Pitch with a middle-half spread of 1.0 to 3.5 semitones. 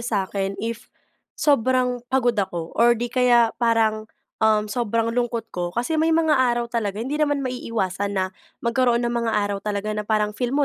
Yes: average, 2.9 semitones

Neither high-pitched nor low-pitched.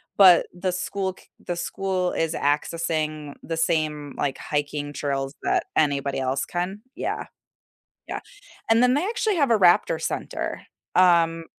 Yes: medium, 165 Hz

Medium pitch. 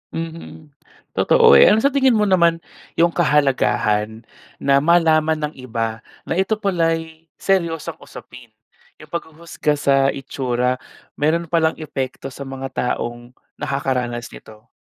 Yes: medium, 155 Hz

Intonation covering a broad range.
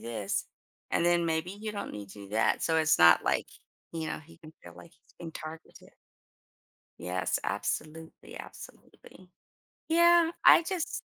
Yes: wide, 8.9 semitones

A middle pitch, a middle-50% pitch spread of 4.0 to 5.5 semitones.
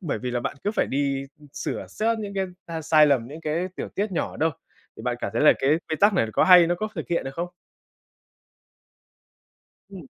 Yes: medium, 165 Hz; average, 5.2 semitones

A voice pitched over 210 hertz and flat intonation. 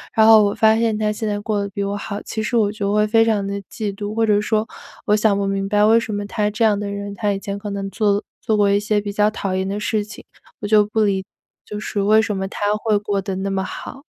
No: high, 205 Hz; narrow, 1.2 semitones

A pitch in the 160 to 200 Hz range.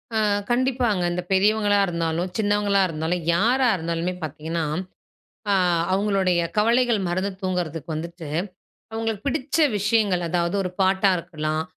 Yes: high, 190 Hz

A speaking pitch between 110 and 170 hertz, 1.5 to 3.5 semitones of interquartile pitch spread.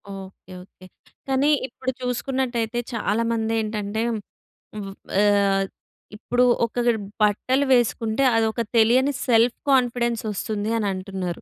No: high, 225 Hz; average, 2.9 semitones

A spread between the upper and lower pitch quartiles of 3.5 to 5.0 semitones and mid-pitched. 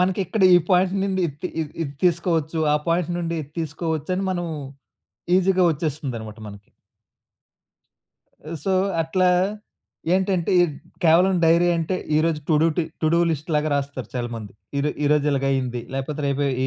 Yes: average, 4.1 semitones; medium, 160 Hz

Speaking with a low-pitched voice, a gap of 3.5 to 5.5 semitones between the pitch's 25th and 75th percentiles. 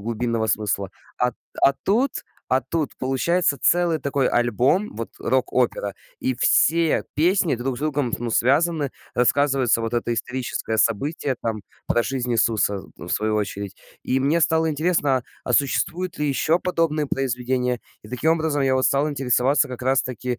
Yes: low, 130 Hz; average, 4.1 semitones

